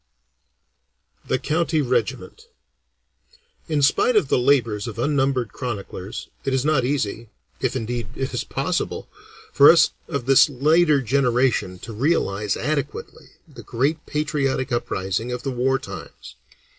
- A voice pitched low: Yes, low, 130 Hz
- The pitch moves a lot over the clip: No, average, 3.5 semitones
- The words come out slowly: Yes, slow, 130 wpm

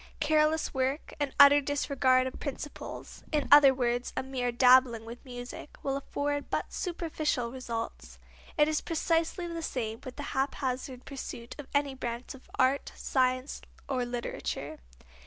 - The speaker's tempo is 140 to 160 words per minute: Yes, average, 145 wpm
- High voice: Yes, very high, 265 Hz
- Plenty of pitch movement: No, narrow, 2.6 semitones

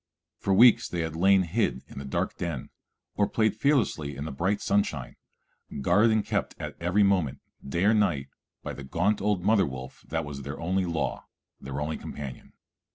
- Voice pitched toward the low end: Yes, very low, 85 Hz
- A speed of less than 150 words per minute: No, average, 185 wpm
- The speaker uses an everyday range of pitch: No, wide, 6.2 semitones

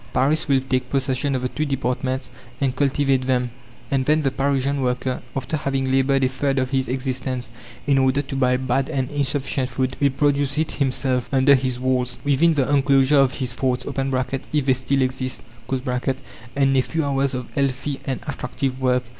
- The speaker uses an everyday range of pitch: No, narrow, 1.4 semitones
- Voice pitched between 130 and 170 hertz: Yes, low, 135 Hz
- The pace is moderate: Yes, average, 185 wpm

